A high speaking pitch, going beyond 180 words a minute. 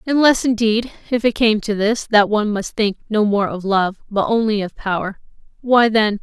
No: high, 215 Hz; average, 175 wpm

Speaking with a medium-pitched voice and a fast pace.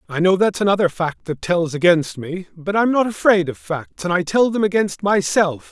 Yes: medium, 180 Hz; fast, 220 wpm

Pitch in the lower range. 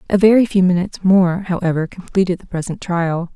No: medium, 185 Hz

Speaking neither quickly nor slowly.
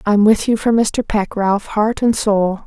No: fast, 225 wpm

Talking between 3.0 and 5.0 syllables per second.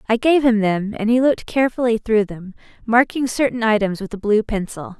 No: 5.6 syllables/s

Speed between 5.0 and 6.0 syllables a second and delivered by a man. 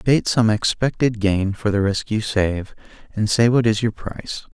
No: 4.5 syllables/s; male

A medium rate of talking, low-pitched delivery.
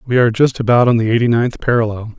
No: fast, 250 wpm; low, 115 Hz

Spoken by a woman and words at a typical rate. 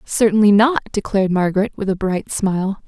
Yes: female; average, 165 wpm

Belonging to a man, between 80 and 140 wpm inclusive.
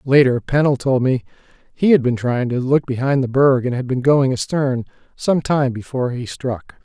No: male; average, 200 wpm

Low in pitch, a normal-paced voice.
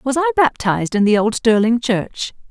No: high, 235 Hz; average, 190 wpm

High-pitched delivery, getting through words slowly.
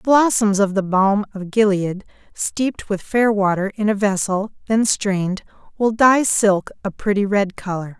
No: high, 205 Hz; average, 175 wpm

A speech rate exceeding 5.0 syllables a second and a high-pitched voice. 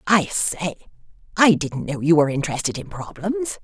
No: 5.3 syllables/s; medium, 175 Hz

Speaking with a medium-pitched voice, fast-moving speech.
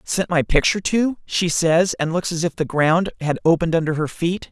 Yes: medium, 170 Hz; fast, 225 wpm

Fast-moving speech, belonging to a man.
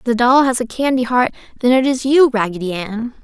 No: fast, 240 wpm; female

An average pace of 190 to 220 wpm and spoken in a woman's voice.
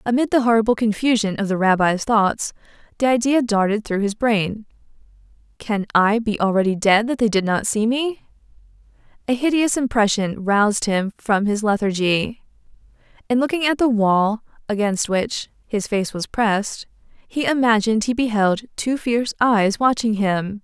No: average, 155 wpm; female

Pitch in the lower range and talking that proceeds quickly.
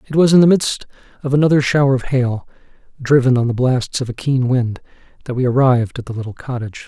Yes: low, 130 Hz; fast, 220 wpm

